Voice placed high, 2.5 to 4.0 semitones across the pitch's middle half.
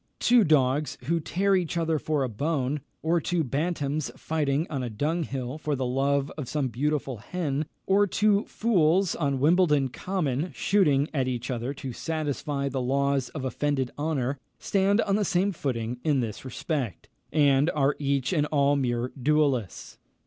No: medium, 145 Hz; average, 3.4 semitones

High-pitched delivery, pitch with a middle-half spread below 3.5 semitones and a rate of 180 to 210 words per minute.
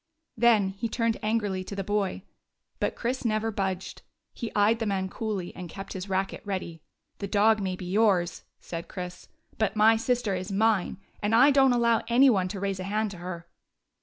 Yes: high, 205 Hz; average, 3.0 semitones; average, 190 wpm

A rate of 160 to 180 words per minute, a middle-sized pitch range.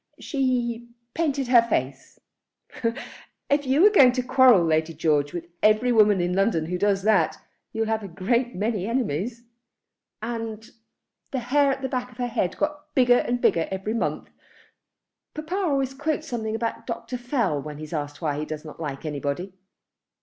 No: average, 165 wpm; wide, 6.4 semitones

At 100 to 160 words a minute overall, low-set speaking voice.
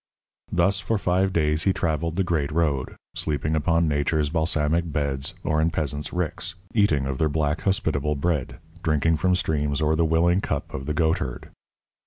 No: average, 170 wpm; very low, 80 Hz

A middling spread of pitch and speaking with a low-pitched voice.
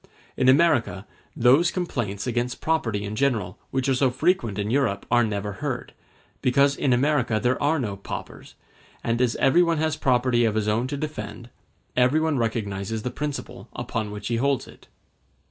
Yes: average, 4.5 semitones; low, 125 Hz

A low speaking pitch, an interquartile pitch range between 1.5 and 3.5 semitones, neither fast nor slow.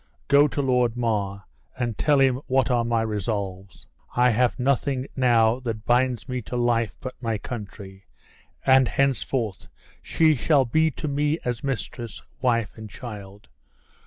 Yes: low, 120 Hz; average, 3.2 semitones; average, 150 wpm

